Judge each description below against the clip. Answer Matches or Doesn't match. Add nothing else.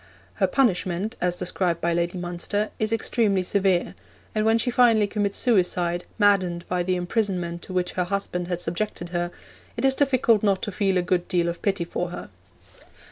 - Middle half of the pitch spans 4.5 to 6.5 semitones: Doesn't match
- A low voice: Doesn't match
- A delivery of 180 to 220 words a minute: Matches